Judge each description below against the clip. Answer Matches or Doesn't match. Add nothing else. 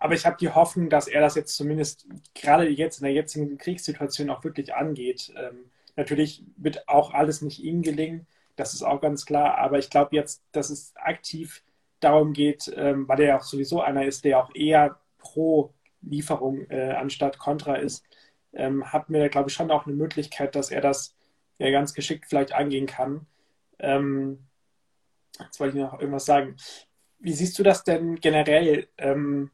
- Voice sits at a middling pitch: Matches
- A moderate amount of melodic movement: Doesn't match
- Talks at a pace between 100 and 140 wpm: Doesn't match